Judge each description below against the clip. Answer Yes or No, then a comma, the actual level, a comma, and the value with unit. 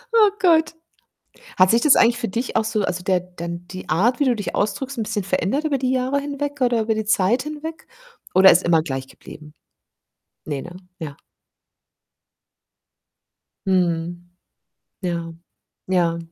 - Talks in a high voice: Yes, high, 205 Hz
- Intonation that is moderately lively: No, wide, 6.9 semitones